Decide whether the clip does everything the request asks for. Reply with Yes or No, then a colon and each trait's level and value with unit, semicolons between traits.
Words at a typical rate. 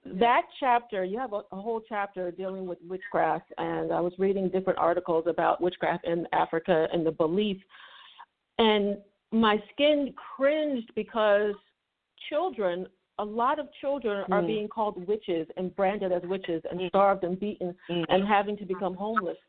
Yes: average, 155 wpm